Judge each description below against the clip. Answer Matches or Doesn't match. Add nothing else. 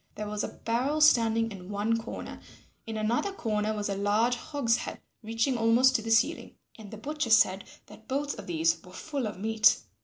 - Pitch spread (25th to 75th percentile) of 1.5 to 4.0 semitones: Matches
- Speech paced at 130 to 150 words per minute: Doesn't match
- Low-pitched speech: Doesn't match